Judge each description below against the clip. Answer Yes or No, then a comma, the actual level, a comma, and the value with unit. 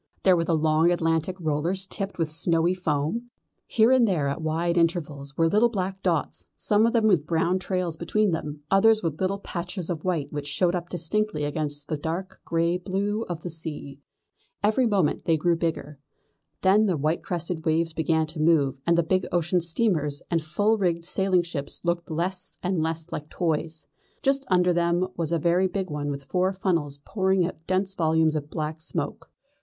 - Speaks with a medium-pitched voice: Yes, medium, 170 Hz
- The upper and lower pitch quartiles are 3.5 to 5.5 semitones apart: No, average, 3.0 semitones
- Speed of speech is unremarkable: Yes, average, 190 wpm